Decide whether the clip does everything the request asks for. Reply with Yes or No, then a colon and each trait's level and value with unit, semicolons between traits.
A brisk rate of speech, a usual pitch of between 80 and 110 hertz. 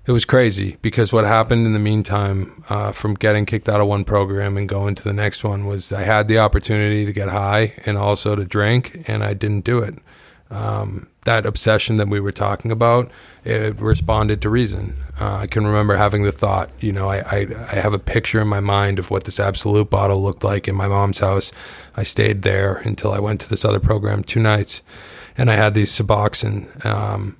Yes: fast, 215 wpm; low, 105 Hz